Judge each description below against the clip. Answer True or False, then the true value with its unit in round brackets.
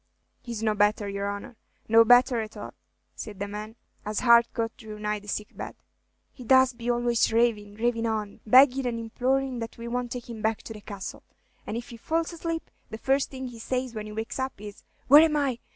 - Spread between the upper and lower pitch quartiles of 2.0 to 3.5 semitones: True (2.9 semitones)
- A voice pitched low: False (230 Hz)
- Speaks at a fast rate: True (215 wpm)